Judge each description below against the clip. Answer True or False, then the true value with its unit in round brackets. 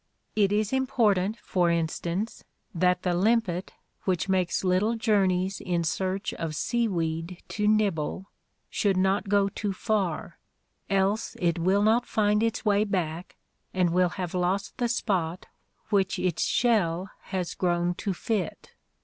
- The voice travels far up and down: False (2.9 semitones)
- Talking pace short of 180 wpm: True (140 wpm)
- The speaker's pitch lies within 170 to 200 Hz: True (190 Hz)